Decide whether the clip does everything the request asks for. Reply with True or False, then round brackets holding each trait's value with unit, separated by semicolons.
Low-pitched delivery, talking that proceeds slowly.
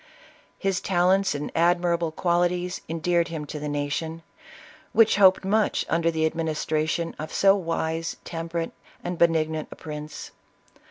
False (165 Hz; 130 wpm)